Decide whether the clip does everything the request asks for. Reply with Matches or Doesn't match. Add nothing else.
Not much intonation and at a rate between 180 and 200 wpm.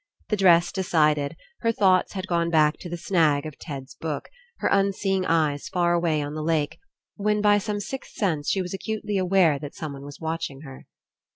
Doesn't match